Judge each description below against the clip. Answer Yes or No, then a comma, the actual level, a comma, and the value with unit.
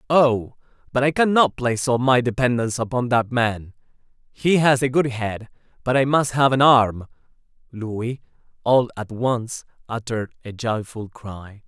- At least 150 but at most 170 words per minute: Yes, average, 155 wpm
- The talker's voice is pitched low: Yes, low, 120 Hz